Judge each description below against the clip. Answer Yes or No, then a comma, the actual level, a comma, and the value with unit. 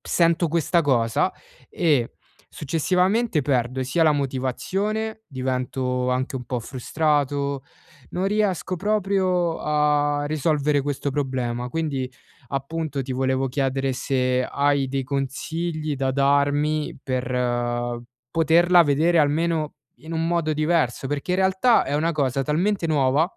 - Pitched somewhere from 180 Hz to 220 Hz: No, medium, 145 Hz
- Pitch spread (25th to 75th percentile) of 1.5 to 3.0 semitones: No, average, 3.9 semitones